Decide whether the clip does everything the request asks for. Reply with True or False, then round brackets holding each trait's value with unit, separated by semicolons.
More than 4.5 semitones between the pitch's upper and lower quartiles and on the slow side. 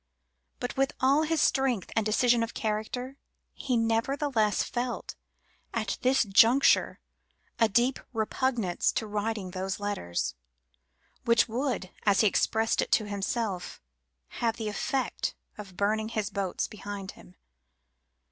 False (3.3 semitones; 130 wpm)